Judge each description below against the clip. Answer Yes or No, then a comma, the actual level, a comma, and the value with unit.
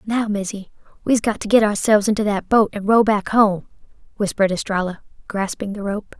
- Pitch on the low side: No, high, 205 Hz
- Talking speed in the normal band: Yes, average, 185 wpm